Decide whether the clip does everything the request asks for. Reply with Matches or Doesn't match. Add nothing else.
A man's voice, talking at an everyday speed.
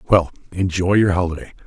Matches